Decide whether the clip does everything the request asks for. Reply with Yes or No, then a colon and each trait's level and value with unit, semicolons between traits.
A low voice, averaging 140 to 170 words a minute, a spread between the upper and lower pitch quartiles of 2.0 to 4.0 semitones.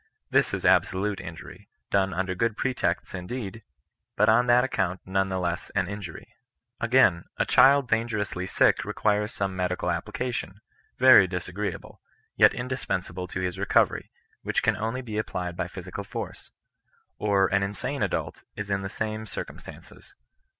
Yes: low, 100 Hz; average, 155 wpm; average, 3.4 semitones